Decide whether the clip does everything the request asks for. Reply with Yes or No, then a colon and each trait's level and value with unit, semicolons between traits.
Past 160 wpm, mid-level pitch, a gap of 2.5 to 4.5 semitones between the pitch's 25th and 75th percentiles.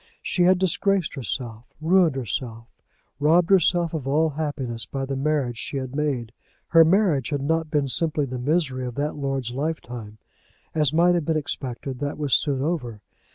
Yes: average, 170 wpm; medium, 145 Hz; average, 3.9 semitones